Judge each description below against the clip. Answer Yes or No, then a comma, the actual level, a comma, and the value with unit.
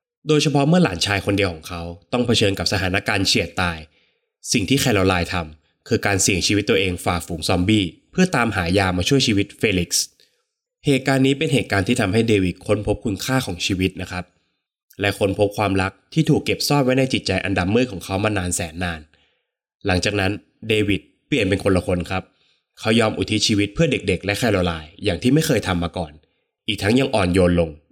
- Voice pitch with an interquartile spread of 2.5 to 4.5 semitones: No, average, 5.0 semitones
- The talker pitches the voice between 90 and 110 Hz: Yes, low, 100 Hz